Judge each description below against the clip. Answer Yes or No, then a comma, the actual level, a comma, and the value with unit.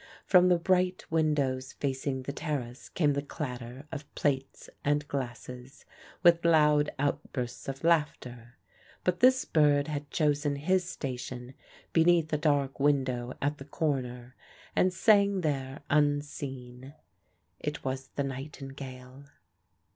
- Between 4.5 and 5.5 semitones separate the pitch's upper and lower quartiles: No, average, 2.8 semitones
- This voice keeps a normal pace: No, slow, 125 wpm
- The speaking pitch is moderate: Yes, medium, 145 Hz